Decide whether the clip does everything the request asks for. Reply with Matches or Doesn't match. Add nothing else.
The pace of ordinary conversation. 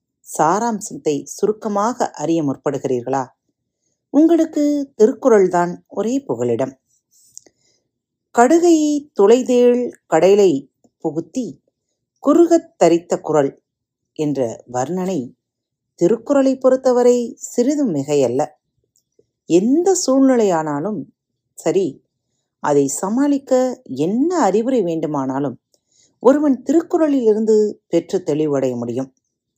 Doesn't match